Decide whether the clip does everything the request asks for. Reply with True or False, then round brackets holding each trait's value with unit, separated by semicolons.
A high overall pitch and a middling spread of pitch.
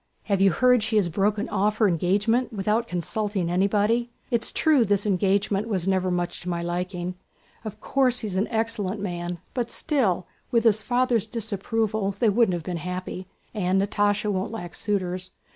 True (205 Hz; 3.4 semitones)